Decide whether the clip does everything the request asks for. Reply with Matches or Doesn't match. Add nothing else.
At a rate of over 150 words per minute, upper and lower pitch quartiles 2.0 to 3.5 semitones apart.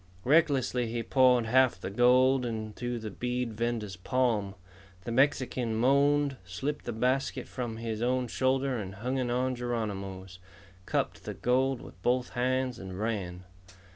Doesn't match